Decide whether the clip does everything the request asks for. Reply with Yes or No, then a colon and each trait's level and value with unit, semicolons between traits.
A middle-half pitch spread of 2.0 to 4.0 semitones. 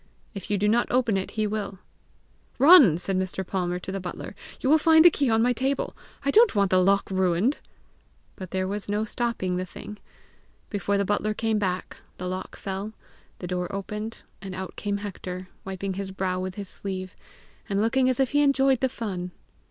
Yes: average, 3.5 semitones